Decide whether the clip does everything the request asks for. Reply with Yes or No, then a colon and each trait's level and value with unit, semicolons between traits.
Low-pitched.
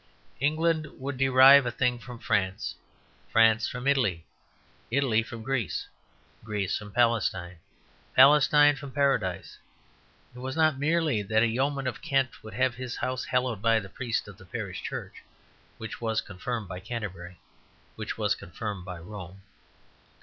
Yes: low, 120 Hz